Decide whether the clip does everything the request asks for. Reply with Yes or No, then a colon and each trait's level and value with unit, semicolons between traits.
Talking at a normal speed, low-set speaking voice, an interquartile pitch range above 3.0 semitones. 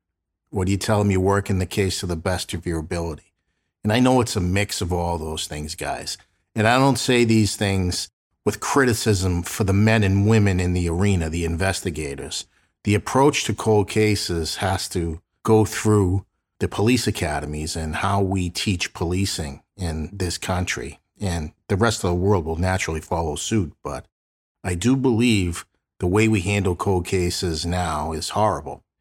Yes: average, 180 wpm; very low, 95 Hz; average, 3.6 semitones